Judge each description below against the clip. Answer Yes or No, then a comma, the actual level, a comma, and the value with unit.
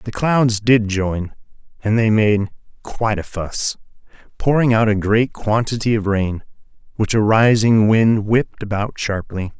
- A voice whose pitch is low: Yes, low, 110 Hz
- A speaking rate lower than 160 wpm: Yes, average, 150 wpm